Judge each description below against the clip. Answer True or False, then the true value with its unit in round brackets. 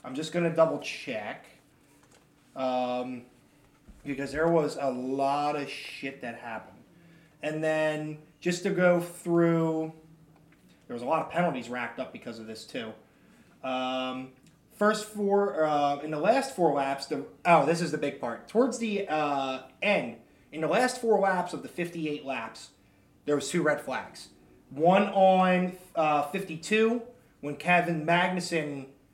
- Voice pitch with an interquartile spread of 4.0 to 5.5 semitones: True (4.4 semitones)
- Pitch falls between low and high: True (155 Hz)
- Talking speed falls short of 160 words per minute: True (150 wpm)